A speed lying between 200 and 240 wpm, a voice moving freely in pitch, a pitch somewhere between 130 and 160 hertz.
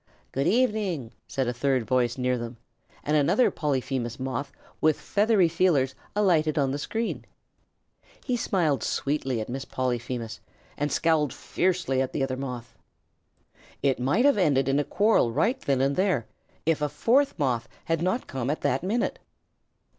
No: average, 160 wpm; wide, 5.8 semitones; medium, 140 Hz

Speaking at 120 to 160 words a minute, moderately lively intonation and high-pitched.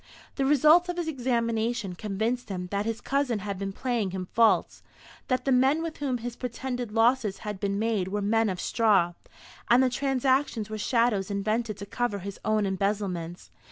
No: average, 180 wpm; average, 4.0 semitones; high, 225 Hz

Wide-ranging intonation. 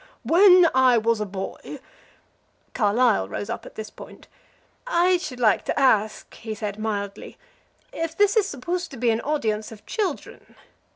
Yes: wide, 7.8 semitones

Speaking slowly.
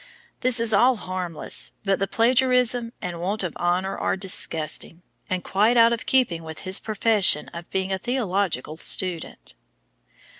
No: average, 150 wpm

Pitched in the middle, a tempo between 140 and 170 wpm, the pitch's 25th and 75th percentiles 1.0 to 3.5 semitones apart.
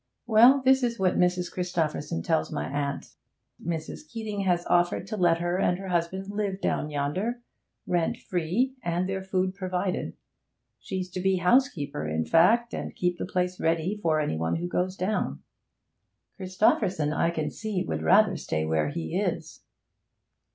Yes: medium, 180 Hz; average, 160 wpm; average, 3.1 semitones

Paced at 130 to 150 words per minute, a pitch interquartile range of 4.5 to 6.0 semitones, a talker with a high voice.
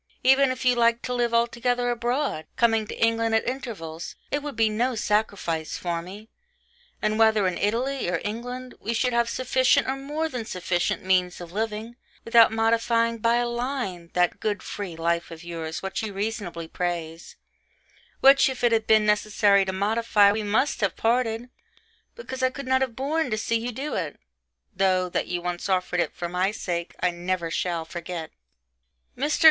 No: average, 180 wpm; average, 5.1 semitones; high, 220 Hz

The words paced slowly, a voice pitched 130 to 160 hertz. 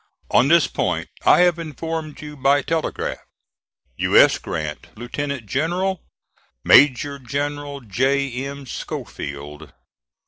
Yes: slow, 110 wpm; medium, 140 Hz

